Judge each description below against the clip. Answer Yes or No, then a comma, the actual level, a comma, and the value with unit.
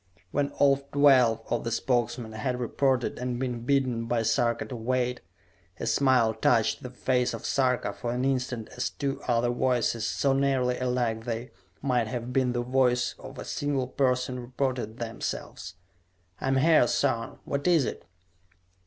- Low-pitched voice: Yes, low, 125 Hz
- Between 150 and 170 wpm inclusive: Yes, average, 160 wpm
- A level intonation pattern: Yes, narrow, 2.0 semitones